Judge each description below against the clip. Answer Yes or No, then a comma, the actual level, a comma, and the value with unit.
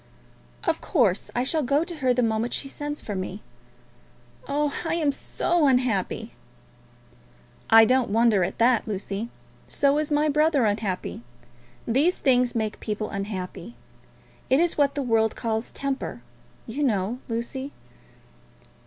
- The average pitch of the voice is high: Yes, high, 245 Hz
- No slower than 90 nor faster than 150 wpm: Yes, average, 140 wpm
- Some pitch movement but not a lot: Yes, average, 4.6 semitones